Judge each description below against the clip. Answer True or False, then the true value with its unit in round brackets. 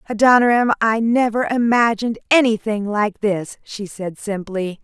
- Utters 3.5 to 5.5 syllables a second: True (4.6 syllables/s)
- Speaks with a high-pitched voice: True (220 Hz)